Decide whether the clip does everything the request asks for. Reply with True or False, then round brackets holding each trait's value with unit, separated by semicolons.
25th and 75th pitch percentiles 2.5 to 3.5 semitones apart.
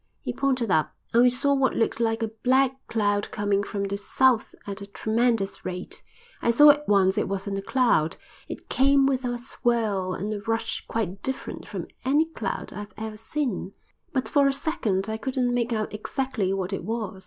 False (4.6 semitones)